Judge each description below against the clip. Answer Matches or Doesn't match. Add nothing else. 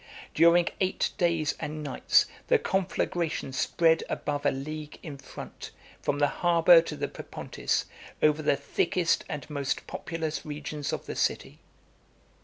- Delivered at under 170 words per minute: Matches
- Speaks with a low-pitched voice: Doesn't match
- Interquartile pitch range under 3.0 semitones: Matches